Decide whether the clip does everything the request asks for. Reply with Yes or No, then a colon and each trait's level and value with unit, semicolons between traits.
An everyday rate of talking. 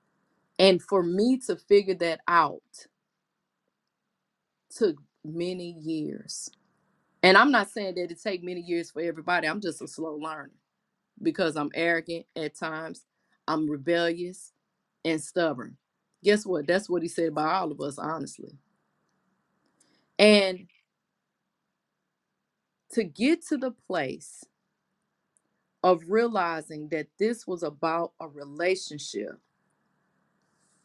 No: slow, 115 wpm